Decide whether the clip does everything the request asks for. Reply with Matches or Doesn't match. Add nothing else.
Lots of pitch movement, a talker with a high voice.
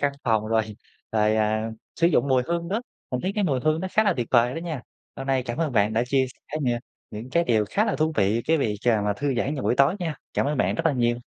Doesn't match